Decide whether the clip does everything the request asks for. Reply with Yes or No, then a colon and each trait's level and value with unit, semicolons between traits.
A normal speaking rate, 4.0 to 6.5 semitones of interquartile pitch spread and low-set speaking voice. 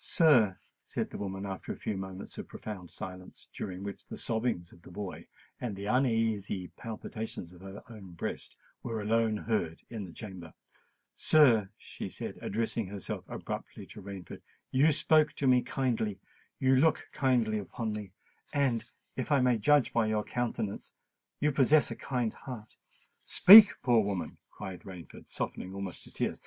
Yes: average, 155 wpm; average, 4.4 semitones; low, 110 Hz